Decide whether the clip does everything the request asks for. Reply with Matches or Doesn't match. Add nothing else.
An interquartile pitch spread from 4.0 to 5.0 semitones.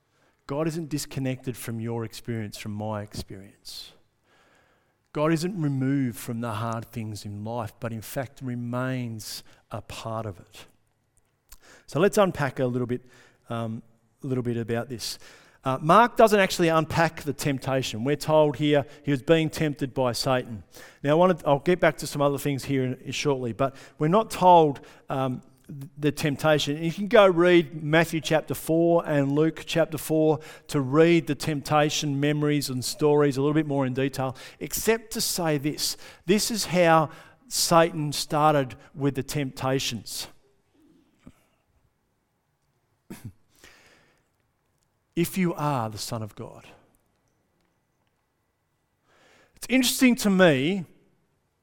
Matches